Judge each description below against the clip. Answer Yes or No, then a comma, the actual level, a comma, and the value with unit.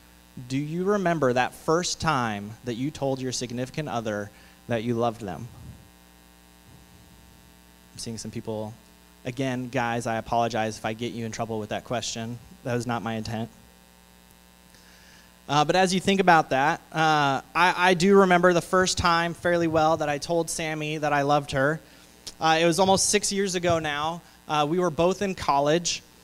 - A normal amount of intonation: No, wide, 7.6 semitones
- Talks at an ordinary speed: Yes, average, 175 wpm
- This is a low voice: Yes, low, 125 Hz